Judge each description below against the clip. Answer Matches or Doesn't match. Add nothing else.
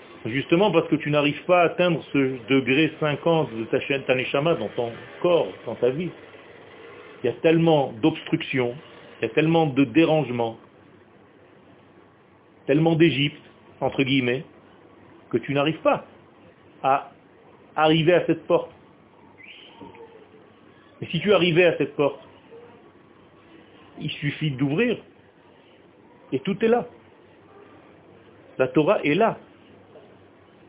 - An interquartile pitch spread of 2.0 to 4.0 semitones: Matches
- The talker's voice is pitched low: Doesn't match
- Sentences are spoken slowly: Matches